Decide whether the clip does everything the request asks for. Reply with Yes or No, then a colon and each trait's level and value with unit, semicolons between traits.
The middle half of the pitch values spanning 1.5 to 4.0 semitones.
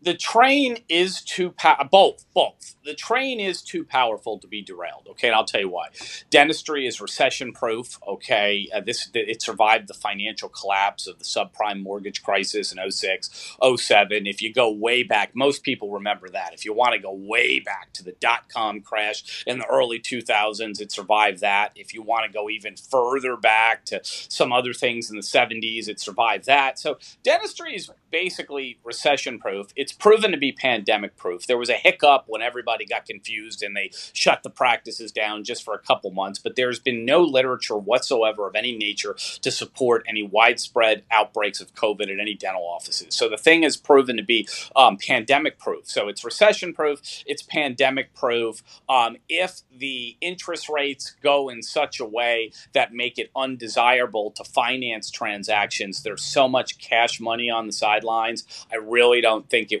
No: wide, 5.4 semitones